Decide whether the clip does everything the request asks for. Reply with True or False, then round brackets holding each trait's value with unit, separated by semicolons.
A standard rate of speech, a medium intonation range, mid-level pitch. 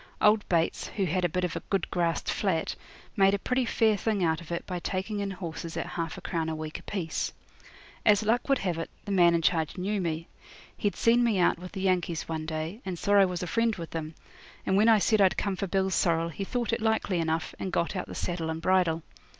False (245 wpm; 3.5 semitones; 180 Hz)